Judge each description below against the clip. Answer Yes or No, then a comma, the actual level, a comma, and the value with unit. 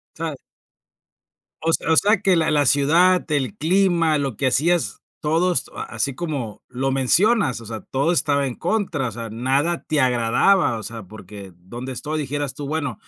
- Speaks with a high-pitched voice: No, medium, 145 Hz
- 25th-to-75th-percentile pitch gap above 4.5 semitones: Yes, average, 5.1 semitones